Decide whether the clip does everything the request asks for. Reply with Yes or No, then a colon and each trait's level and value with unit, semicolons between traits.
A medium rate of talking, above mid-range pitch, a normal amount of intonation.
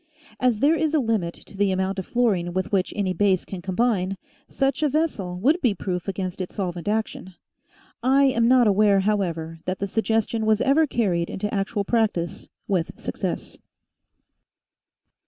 Yes: average, 165 wpm; high, 205 Hz; average, 4.2 semitones